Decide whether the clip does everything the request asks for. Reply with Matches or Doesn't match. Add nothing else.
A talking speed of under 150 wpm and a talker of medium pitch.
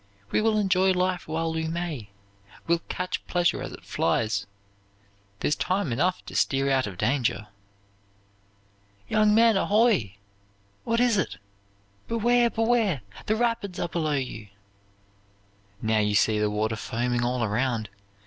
Matches